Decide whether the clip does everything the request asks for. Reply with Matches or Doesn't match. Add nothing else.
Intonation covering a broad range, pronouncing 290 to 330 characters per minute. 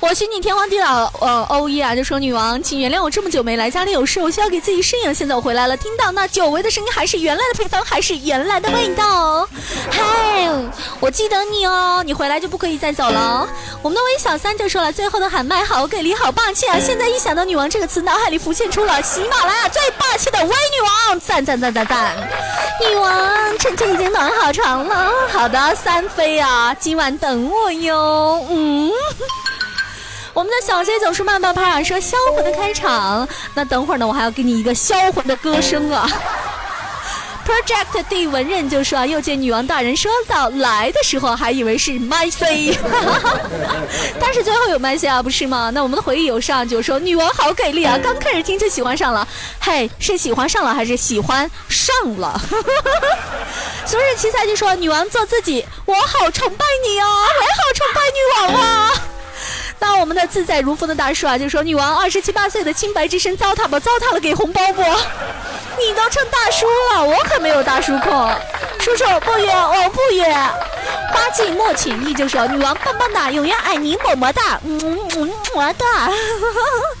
Matches